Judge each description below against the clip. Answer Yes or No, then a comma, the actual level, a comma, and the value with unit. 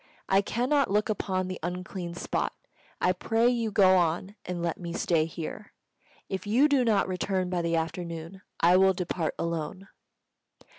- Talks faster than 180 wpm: No, average, 160 wpm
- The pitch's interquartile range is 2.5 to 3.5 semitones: Yes, average, 3.0 semitones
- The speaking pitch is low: No, medium, 185 Hz